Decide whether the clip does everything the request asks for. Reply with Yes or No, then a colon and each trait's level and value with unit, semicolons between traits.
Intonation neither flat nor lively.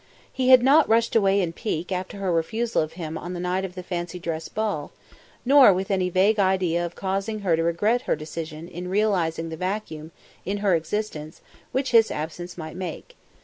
Yes: average, 4.0 semitones